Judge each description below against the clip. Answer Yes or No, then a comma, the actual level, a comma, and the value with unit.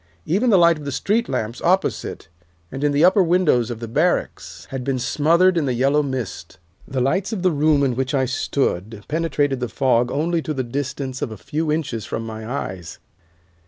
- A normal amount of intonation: Yes, average, 5.0 semitones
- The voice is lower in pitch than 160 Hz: Yes, medium, 140 Hz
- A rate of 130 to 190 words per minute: No, average, 200 wpm